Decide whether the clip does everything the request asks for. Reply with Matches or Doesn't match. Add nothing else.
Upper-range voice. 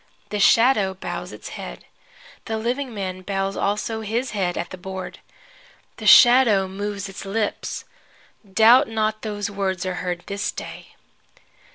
Matches